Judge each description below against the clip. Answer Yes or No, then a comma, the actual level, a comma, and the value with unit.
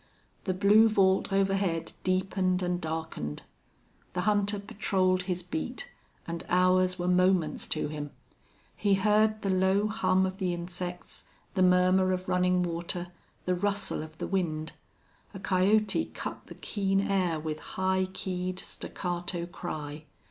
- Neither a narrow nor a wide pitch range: No, narrow, 1.8 semitones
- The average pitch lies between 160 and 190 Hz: Yes, medium, 185 Hz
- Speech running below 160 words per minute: Yes, average, 140 wpm